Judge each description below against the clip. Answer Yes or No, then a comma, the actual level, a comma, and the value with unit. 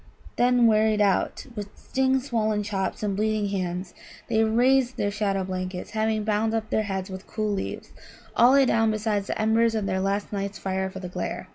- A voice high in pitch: Yes, high, 210 Hz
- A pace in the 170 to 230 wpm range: Yes, average, 195 wpm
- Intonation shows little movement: Yes, narrow, 2.3 semitones